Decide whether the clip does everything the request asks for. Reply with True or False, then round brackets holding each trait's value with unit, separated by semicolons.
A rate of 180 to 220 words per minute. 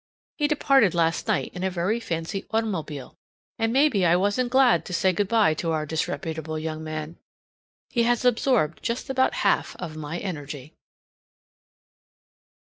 False (150 wpm)